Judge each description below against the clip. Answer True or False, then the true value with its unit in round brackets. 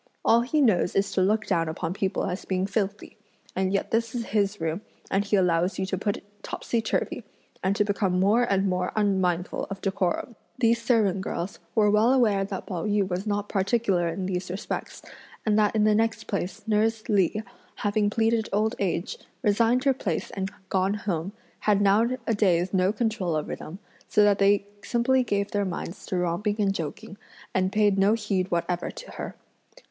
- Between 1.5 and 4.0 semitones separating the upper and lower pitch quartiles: True (2.6 semitones)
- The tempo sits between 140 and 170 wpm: False (185 wpm)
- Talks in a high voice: True (200 Hz)